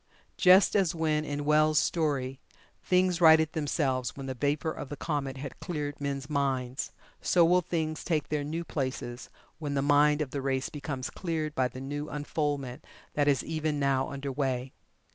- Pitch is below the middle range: No, medium, 145 Hz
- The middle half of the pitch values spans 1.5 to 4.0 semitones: Yes, narrow, 2.5 semitones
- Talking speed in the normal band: Yes, average, 175 wpm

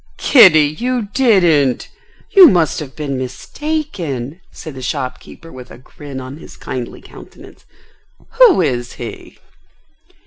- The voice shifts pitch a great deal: Yes, wide, 8.7 semitones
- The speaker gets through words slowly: Yes, slow, 125 wpm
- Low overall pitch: No, medium, 155 Hz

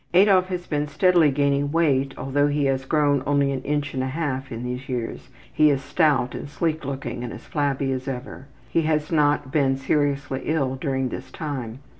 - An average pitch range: No, narrow, 2.2 semitones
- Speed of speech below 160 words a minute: No, average, 195 wpm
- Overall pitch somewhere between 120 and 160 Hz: Yes, medium, 140 Hz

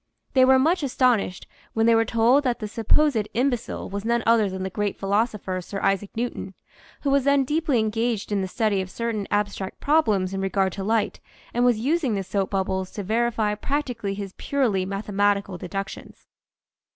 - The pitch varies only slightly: No, average, 3.8 semitones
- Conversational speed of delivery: Yes, average, 185 wpm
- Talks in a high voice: Yes, high, 215 Hz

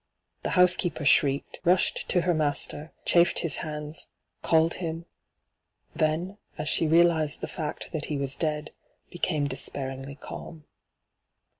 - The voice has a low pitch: No, medium, 155 Hz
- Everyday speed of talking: No, slow, 130 wpm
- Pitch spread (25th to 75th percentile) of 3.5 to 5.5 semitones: No, narrow, 2.6 semitones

